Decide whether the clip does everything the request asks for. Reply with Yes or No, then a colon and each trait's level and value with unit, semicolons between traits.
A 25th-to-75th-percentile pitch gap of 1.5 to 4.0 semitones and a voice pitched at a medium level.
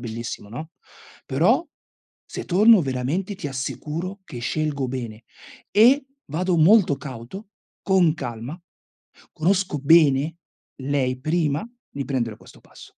No: wide, 6.0 semitones; medium, 150 Hz